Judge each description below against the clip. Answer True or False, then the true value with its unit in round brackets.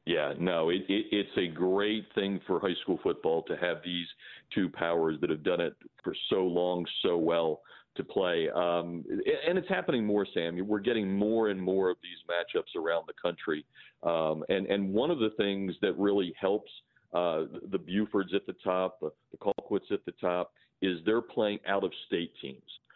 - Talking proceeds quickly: False (190 wpm)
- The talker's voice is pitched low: True (95 Hz)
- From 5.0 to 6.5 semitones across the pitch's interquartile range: False (2.9 semitones)